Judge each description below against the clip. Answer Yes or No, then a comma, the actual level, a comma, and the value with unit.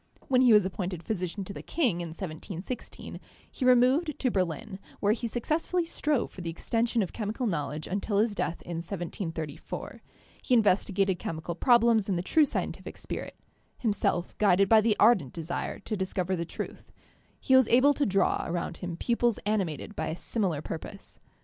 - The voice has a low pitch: No, high, 200 Hz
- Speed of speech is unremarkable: Yes, average, 175 wpm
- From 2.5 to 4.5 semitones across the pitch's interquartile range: No, average, 5.3 semitones